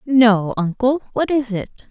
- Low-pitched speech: No, high, 240 Hz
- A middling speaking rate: Yes, average, 155 wpm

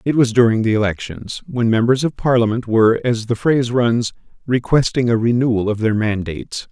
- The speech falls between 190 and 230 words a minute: No, average, 180 wpm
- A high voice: No, low, 120 Hz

